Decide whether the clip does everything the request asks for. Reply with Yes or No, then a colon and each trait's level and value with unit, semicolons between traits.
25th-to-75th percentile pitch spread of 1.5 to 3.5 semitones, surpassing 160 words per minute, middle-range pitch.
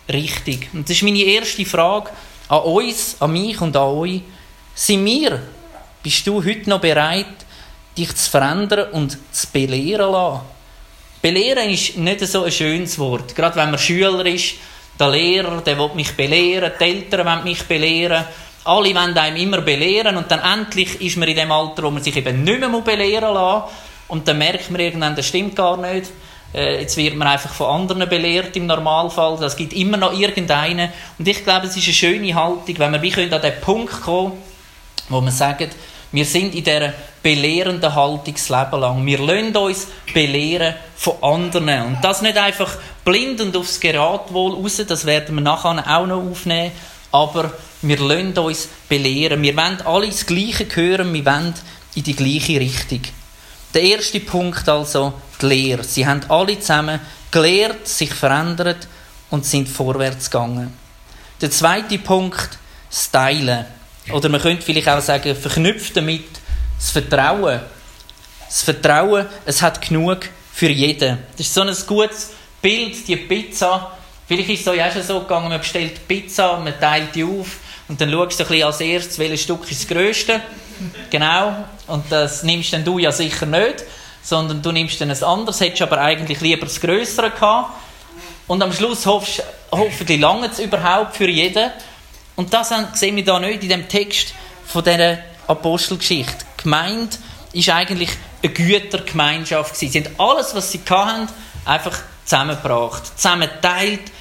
No: average, 3.9 semitones; average, 170 wpm; medium, 170 Hz